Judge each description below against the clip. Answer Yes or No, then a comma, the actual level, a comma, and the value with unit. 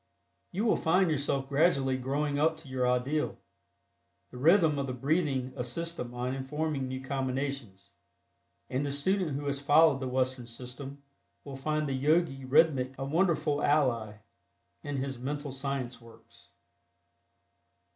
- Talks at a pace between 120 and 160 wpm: Yes, average, 145 wpm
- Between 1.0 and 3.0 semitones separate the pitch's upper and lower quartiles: Yes, narrow, 2.6 semitones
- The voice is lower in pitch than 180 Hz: Yes, medium, 140 Hz